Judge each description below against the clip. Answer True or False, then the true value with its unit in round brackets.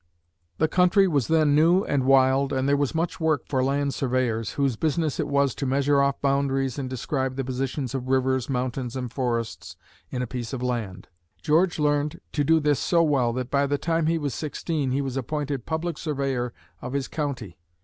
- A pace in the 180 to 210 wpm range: True (200 wpm)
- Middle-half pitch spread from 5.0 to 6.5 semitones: False (2.5 semitones)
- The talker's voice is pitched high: False (140 Hz)